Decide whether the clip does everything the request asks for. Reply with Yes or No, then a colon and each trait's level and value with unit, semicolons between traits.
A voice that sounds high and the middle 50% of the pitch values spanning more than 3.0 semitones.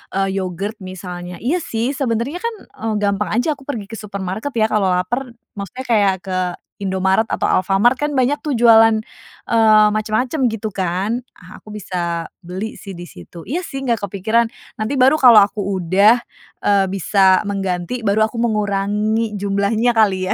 Yes: high, 210 Hz; average, 3.4 semitones